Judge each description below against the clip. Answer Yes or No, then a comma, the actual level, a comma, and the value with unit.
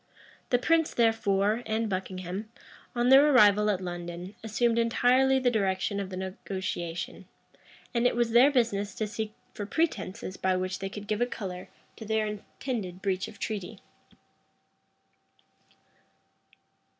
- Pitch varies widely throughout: No, average, 4.0 semitones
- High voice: Yes, high, 210 Hz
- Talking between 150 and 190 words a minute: No, average, 140 wpm